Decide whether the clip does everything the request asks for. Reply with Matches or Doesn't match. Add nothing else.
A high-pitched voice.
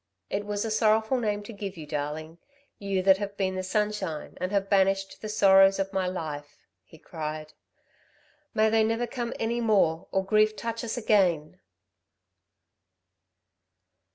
Matches